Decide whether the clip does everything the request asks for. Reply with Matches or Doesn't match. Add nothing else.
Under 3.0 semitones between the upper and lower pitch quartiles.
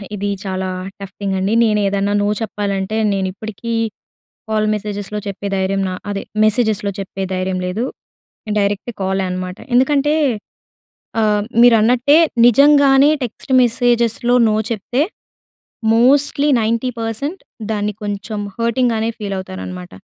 Doesn't match